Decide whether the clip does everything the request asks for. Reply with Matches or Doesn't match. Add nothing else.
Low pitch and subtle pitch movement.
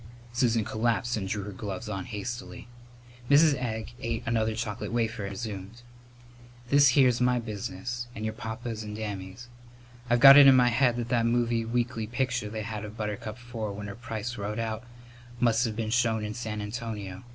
Matches